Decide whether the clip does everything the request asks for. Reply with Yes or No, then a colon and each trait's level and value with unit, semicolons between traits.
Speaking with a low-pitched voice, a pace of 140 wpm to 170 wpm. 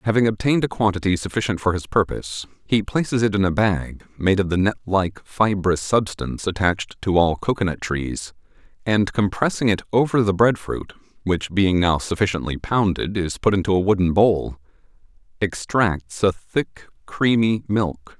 Yes: low, 100 Hz; average, 160 wpm